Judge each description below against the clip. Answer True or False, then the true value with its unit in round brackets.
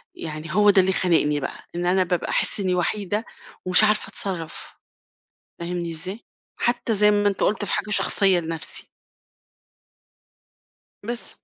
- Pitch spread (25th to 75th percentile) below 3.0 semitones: False (3.4 semitones)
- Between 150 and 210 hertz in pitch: True (185 Hz)